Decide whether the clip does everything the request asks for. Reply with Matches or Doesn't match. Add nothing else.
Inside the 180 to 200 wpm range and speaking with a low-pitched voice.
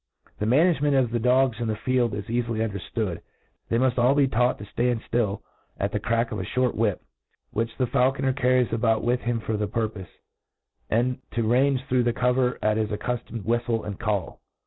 Matches